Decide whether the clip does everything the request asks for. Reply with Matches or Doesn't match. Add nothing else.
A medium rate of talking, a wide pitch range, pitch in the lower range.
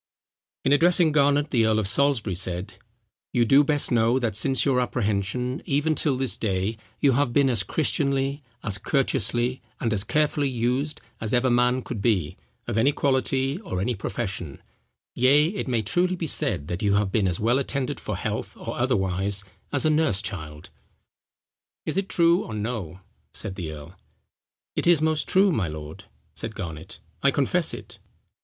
Matches